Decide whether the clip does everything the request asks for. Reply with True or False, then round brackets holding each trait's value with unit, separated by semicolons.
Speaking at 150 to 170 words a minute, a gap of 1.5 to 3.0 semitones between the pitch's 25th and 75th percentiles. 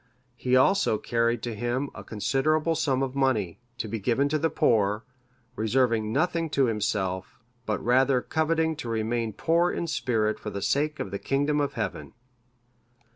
False (165 wpm; 4.8 semitones)